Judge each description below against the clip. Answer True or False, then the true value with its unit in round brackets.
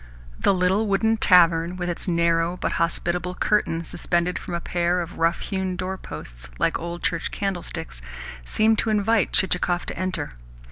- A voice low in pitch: False (180 Hz)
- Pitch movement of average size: False (2.0 semitones)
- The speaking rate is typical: True (155 wpm)